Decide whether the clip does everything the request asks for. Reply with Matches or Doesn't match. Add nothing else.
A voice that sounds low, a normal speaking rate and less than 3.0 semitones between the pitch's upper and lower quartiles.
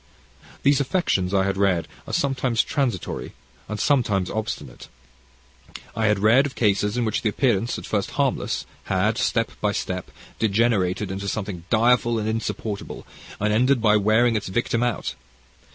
Doesn't match